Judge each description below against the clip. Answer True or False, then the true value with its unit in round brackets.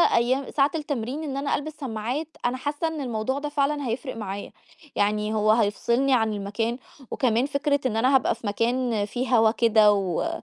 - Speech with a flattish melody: False (4.3 semitones)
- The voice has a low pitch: False (245 Hz)